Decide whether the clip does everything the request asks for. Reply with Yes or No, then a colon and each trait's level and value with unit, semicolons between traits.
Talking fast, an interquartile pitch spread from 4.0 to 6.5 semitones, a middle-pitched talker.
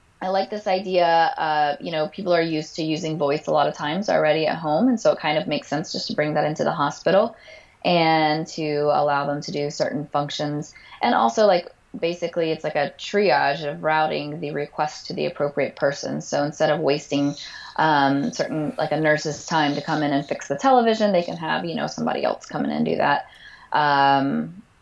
No: fast, 215 wpm; average, 2.7 semitones; medium, 155 Hz